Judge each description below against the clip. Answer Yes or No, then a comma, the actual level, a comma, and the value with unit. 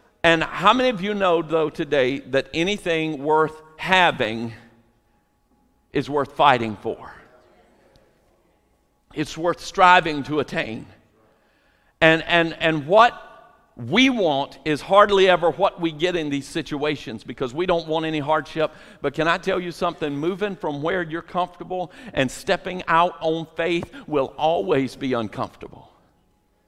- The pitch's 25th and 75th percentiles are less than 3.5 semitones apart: No, average, 3.9 semitones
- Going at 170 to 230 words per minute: No, average, 140 wpm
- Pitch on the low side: No, medium, 160 Hz